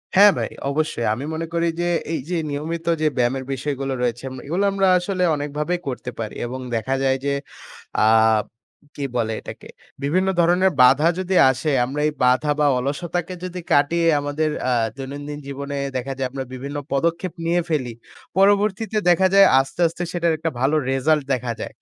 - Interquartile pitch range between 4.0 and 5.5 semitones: Yes, average, 4.4 semitones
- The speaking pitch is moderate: Yes, medium, 150 Hz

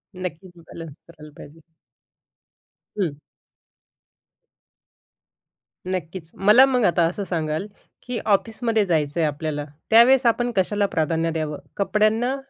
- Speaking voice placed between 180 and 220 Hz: Yes, medium, 185 Hz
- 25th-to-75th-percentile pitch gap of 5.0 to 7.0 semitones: Yes, wide, 5.6 semitones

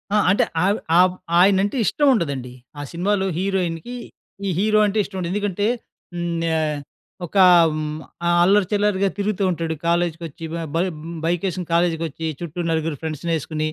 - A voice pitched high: No, medium, 175 Hz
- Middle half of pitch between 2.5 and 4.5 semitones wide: Yes, average, 3.4 semitones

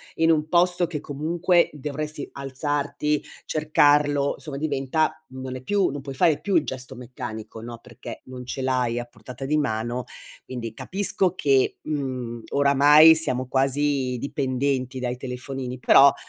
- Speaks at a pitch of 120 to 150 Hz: Yes, low, 135 Hz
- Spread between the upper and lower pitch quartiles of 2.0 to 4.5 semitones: Yes, average, 2.9 semitones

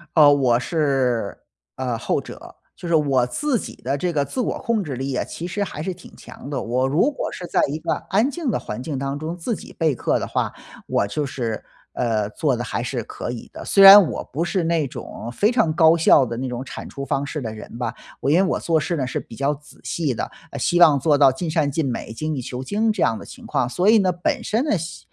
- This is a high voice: No, medium, 145 Hz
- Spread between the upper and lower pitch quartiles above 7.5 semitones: No, wide, 5.4 semitones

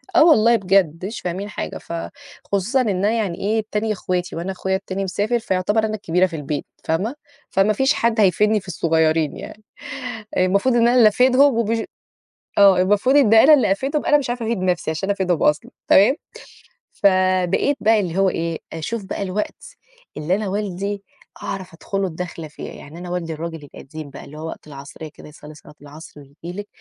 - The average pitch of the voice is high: Yes, high, 195 Hz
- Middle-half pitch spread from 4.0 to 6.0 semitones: Yes, average, 4.5 semitones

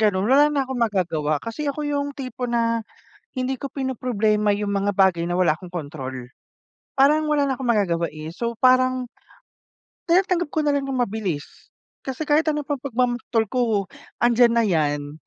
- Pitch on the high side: Yes, high, 235 Hz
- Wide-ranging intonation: Yes, wide, 6.2 semitones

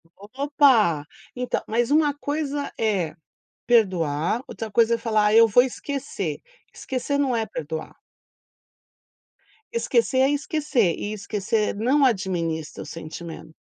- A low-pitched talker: No, high, 225 Hz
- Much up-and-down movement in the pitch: Yes, wide, 6.3 semitones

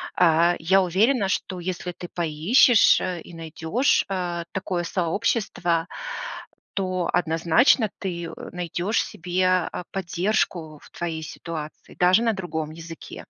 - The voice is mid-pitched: Yes, medium, 175 Hz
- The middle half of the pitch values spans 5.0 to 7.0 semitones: No, narrow, 2.5 semitones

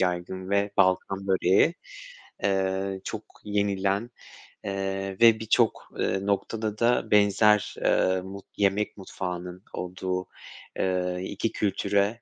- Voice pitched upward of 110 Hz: No, very low, 95 Hz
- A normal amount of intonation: No, narrow, 1.7 semitones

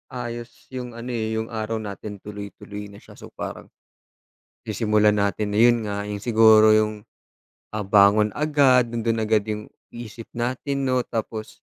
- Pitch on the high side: No, low, 110 Hz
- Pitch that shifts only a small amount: Yes, narrow, 2.2 semitones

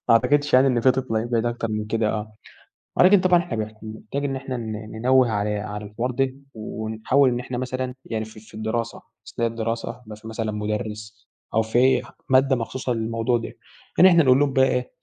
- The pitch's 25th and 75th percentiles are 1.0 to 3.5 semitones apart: Yes, average, 3.0 semitones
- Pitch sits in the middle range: No, low, 115 Hz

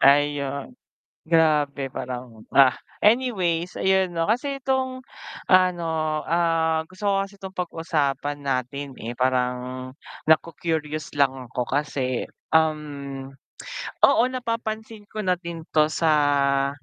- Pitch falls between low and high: Yes, medium, 155 Hz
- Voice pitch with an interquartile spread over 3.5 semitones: Yes, average, 5.1 semitones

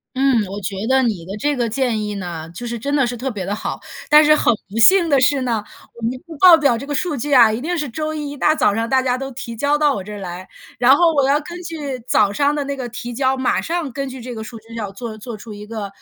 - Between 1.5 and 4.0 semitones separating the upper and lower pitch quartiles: No, average, 4.7 semitones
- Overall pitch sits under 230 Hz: No, very high, 250 Hz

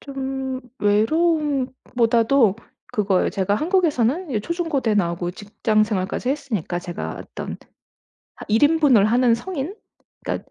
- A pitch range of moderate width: No, wide, 5.8 semitones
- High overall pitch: Yes, high, 245 Hz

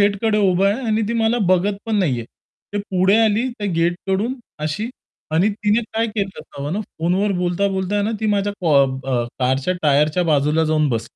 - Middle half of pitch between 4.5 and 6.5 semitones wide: Yes, average, 4.9 semitones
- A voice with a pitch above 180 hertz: Yes, high, 190 Hz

